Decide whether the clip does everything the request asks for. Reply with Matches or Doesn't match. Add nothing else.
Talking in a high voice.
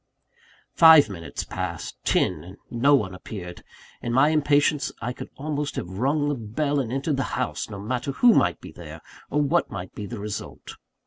Doesn't match